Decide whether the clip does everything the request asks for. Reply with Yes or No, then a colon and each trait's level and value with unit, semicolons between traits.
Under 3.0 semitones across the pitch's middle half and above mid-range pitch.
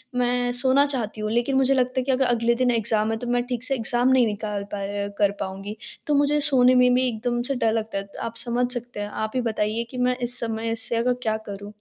Yes: narrow, 2.4 semitones; high, 240 Hz